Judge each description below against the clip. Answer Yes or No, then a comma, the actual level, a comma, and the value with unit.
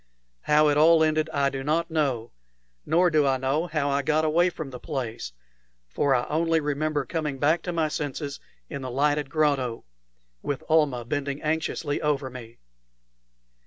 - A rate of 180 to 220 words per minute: No, average, 165 wpm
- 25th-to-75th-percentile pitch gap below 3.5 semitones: Yes, narrow, 2.5 semitones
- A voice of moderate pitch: Yes, medium, 150 Hz